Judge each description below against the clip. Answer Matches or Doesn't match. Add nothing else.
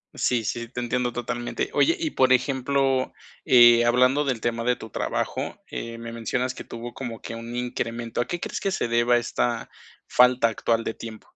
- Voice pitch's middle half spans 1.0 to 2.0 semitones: Matches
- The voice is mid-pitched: Doesn't match